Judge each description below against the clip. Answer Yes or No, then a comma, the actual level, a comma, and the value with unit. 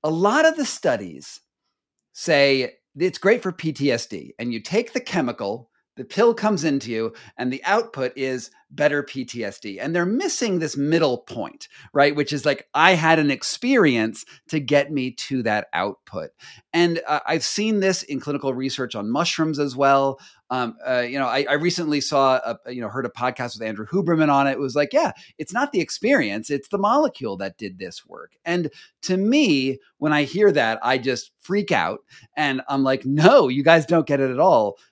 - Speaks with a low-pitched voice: No, medium, 145 Hz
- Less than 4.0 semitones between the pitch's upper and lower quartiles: No, average, 4.4 semitones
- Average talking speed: Yes, average, 195 wpm